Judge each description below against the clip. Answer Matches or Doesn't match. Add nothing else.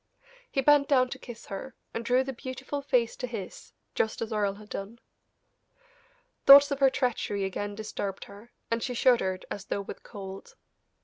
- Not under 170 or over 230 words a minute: Matches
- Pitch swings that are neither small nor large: Matches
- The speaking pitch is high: Matches